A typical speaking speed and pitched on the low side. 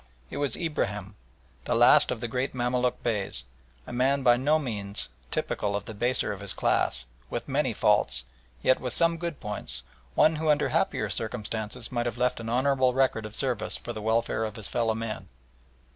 Yes: average, 190 wpm; low, 120 Hz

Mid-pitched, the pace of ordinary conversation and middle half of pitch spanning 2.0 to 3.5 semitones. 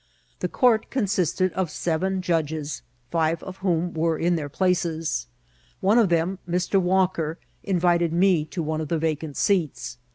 Yes: medium, 170 Hz; average, 155 wpm; average, 2.9 semitones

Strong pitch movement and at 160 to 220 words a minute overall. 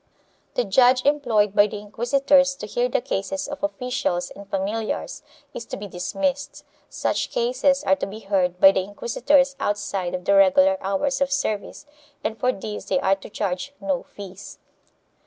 Yes: wide, 6.0 semitones; average, 170 wpm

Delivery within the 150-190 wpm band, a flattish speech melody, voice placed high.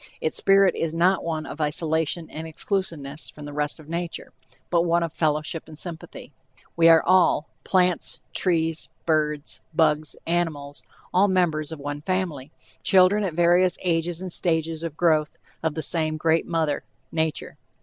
No: average, 160 wpm; narrow, 2.1 semitones; medium, 165 Hz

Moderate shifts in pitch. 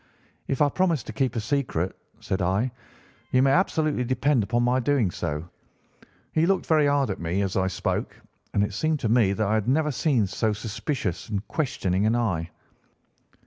No: wide, 6.2 semitones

